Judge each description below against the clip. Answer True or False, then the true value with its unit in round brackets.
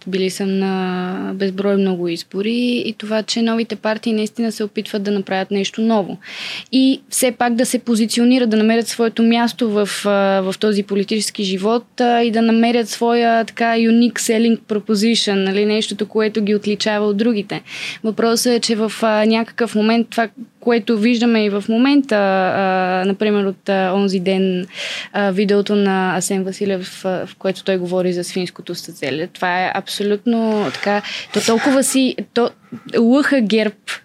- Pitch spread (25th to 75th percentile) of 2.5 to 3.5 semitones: True (2.9 semitones)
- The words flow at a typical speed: True (150 wpm)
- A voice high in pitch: True (215 Hz)